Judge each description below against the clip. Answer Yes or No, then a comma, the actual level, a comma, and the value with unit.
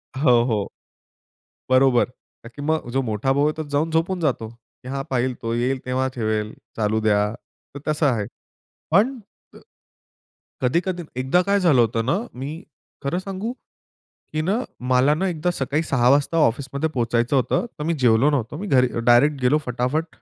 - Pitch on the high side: No, low, 135 Hz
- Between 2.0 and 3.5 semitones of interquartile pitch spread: No, average, 4.7 semitones